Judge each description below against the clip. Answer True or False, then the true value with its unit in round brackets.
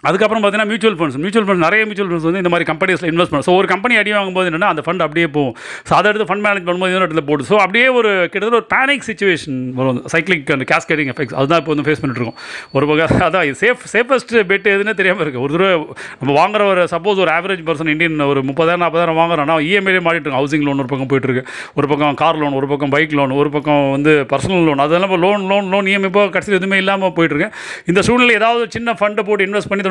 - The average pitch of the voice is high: False (175 Hz)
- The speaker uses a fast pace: True (230 wpm)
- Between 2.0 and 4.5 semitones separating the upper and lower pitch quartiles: False (5.1 semitones)